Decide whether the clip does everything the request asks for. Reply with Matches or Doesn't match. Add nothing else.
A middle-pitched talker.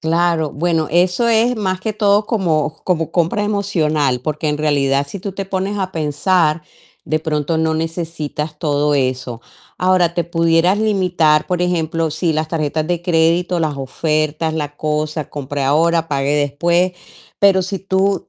Matches